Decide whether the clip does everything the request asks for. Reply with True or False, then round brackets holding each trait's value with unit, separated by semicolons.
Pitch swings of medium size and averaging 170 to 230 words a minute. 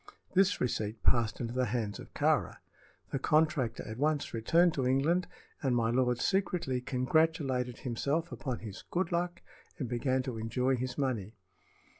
False (4.6 semitones; 155 wpm)